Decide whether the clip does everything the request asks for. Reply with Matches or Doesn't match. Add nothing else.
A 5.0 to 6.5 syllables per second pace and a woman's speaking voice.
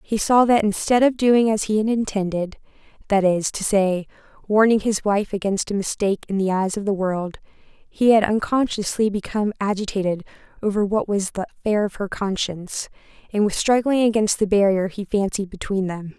Matches